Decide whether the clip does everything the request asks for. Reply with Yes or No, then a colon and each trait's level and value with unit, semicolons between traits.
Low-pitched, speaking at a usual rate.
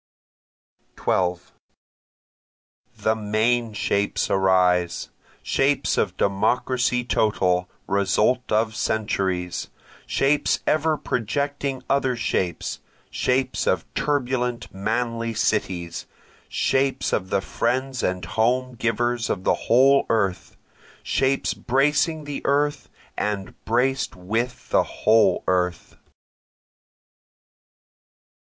No: low, 115 Hz; slow, 90 wpm